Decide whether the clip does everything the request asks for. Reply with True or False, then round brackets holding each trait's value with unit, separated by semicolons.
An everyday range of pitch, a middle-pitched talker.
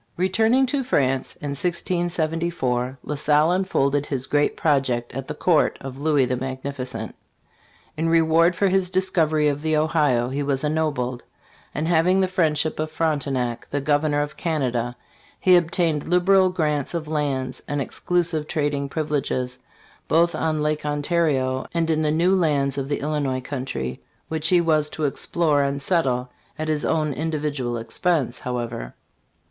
True (3.5 semitones; 150 Hz)